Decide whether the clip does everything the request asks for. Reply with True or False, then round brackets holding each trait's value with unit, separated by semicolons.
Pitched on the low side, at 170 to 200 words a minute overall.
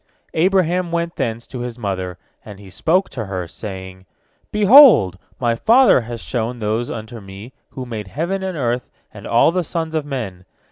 True (120 Hz; 175 wpm)